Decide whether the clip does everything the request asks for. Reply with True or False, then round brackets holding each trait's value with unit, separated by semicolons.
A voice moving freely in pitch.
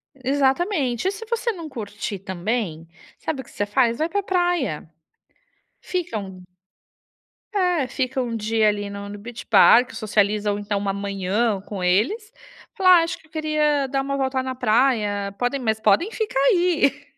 True (7.2 semitones)